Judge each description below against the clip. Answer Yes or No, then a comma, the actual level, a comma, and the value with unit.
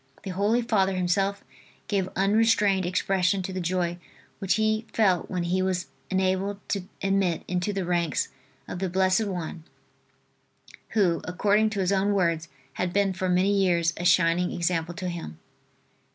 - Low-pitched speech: No, medium, 185 Hz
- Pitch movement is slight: Yes, narrow, 2.0 semitones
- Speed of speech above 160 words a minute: No, average, 155 wpm